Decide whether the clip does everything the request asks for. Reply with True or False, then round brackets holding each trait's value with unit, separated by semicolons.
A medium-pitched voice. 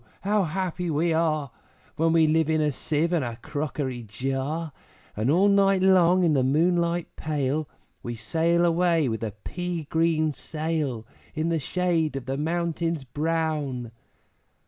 True (160 Hz)